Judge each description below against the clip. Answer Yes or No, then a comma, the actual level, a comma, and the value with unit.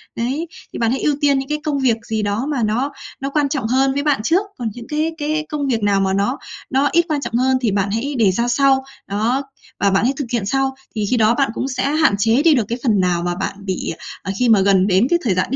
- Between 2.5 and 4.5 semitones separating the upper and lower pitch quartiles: No, average, 5.0 semitones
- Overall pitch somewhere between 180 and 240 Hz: No, very high, 250 Hz